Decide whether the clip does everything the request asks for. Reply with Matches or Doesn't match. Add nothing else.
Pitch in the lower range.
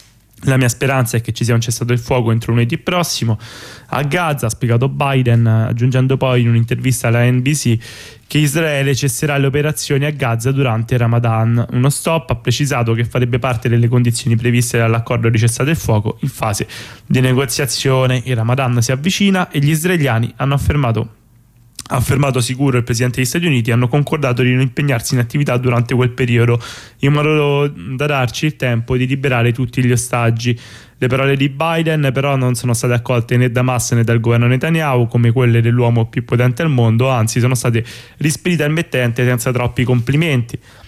Matches